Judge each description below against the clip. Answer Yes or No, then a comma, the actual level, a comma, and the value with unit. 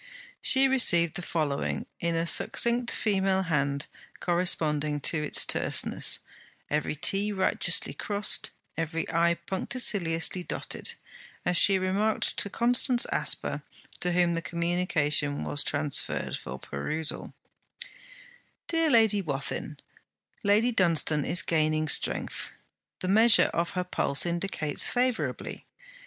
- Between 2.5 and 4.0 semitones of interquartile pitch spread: No, average, 4.7 semitones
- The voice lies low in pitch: No, medium, 175 Hz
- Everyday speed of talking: No, slow, 115 wpm